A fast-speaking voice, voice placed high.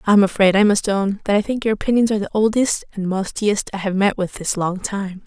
Yes: fast, 250 wpm; high, 200 Hz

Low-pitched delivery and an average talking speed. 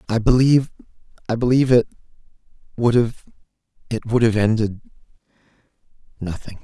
No: low, 115 Hz; slow, 80 wpm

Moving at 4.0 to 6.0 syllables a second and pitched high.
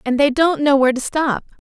Yes: 5.9 syllables/s; very high, 280 Hz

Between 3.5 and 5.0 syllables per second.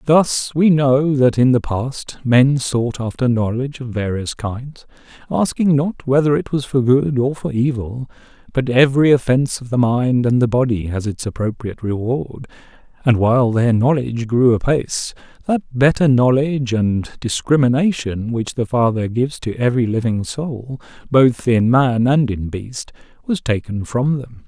Yes: 4.6 syllables/s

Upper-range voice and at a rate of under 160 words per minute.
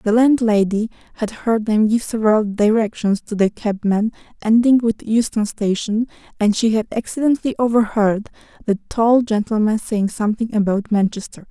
Yes: high, 220 Hz; average, 140 wpm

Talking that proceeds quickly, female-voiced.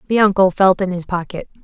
Yes: fast, 220 wpm; female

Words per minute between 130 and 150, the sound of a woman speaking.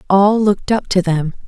No: fast, 205 wpm; female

